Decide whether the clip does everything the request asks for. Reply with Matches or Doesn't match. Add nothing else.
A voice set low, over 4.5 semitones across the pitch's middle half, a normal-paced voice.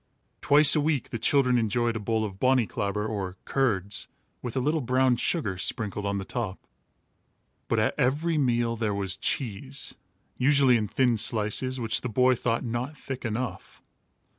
Doesn't match